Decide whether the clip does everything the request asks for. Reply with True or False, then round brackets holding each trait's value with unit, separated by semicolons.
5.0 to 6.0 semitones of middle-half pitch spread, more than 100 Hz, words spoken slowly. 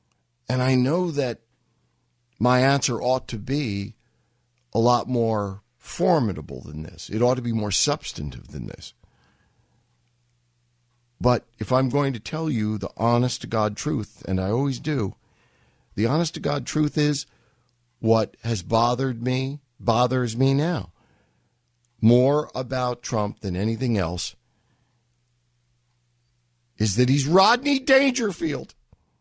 False (2.9 semitones; 120 Hz; 130 wpm)